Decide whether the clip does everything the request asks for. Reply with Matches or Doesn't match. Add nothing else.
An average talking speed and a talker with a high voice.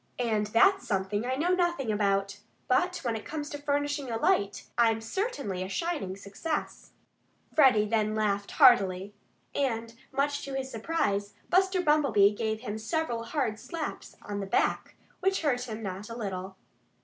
Matches